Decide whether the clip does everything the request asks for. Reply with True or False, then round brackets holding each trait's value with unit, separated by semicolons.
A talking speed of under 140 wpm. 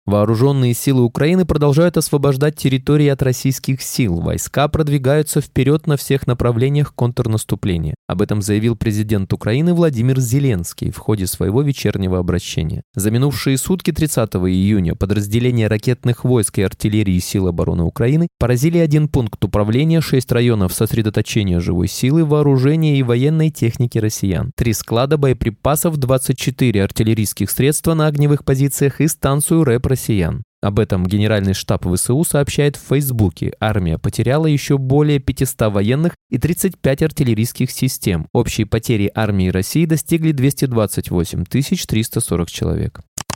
True (130 wpm)